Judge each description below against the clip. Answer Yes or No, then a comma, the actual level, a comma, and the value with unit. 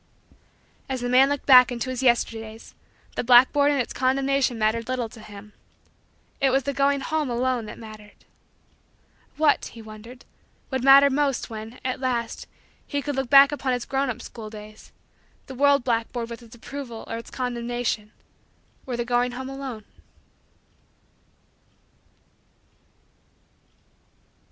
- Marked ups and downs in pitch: No, average, 2.8 semitones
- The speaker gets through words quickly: No, average, 140 wpm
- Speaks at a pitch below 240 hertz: No, very high, 250 Hz